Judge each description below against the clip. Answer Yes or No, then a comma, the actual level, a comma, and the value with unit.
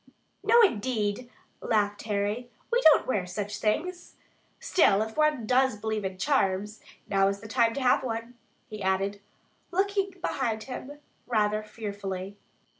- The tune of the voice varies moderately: Yes, average, 4.3 semitones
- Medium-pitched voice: No, high, 220 Hz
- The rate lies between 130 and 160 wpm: Yes, average, 140 wpm